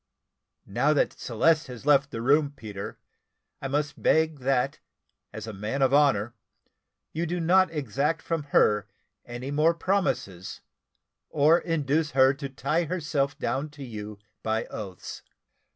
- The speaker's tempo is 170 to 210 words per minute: No, average, 140 wpm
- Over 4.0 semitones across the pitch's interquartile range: Yes, average, 4.4 semitones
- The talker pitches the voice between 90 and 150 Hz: Yes, medium, 140 Hz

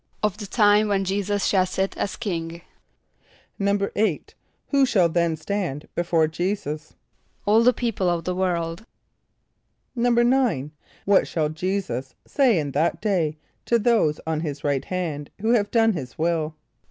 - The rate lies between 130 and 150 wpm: Yes, average, 145 wpm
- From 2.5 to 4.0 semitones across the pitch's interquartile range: No, average, 4.6 semitones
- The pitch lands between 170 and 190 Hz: Yes, medium, 185 Hz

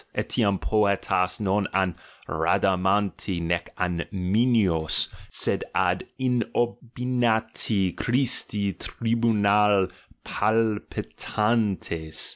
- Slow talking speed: Yes, slow, 75 wpm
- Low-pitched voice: Yes, low, 105 Hz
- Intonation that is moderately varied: Yes, average, 3.6 semitones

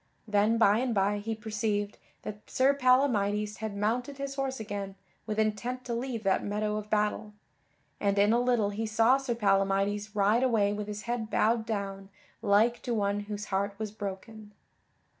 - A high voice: Yes, high, 215 Hz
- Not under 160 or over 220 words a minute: Yes, average, 175 wpm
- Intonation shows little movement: Yes, narrow, 2.3 semitones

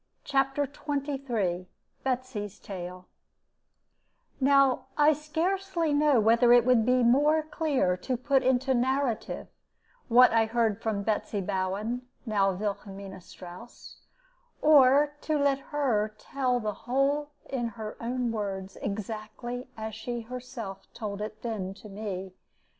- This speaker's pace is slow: Yes, slow, 125 wpm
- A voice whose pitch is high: Yes, high, 240 Hz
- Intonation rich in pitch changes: No, average, 4.6 semitones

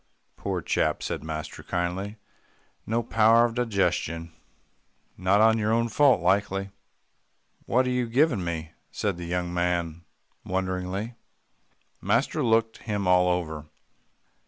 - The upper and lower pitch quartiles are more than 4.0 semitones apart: Yes, average, 4.4 semitones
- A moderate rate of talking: No, slow, 120 wpm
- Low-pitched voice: Yes, very low, 95 Hz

